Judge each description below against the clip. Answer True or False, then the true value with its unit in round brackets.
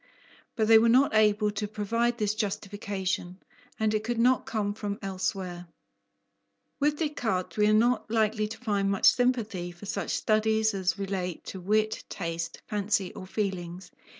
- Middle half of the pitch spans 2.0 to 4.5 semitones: True (2.4 semitones)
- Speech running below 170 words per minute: True (155 wpm)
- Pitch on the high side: True (210 Hz)